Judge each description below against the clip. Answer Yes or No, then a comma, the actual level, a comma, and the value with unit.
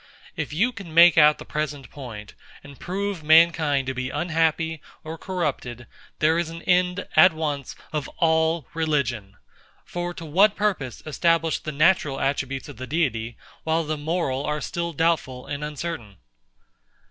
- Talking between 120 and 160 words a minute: Yes, average, 155 wpm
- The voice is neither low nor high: Yes, medium, 155 Hz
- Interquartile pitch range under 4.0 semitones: Yes, average, 3.4 semitones